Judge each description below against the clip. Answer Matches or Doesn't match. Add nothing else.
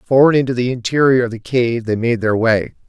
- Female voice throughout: Doesn't match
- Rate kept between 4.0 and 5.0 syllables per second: Doesn't match